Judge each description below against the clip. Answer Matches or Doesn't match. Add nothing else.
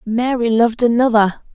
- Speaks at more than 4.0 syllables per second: Matches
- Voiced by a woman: Matches